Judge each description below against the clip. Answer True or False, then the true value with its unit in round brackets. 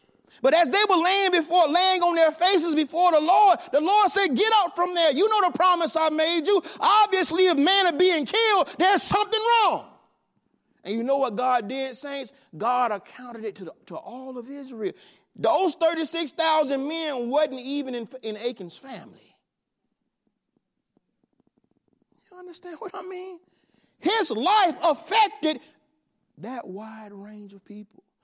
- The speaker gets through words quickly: False (160 wpm)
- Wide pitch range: True (6.7 semitones)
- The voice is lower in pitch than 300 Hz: False (315 Hz)